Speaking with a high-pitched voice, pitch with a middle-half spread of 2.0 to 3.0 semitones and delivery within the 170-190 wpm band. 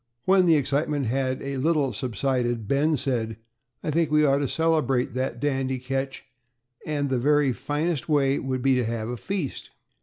No: low, 135 Hz; average, 2.7 semitones; average, 175 wpm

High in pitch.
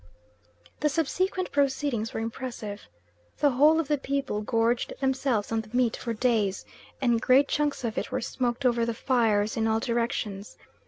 Yes: high, 240 Hz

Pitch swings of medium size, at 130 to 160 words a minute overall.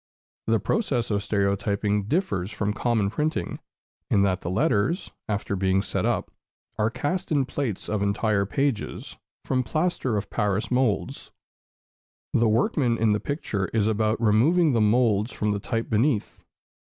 Yes: average, 4.0 semitones; average, 150 wpm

